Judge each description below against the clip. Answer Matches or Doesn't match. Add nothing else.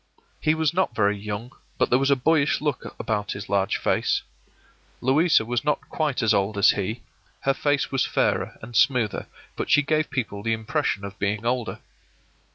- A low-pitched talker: Matches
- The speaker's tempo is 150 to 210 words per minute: Matches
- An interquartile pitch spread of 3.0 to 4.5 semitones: Doesn't match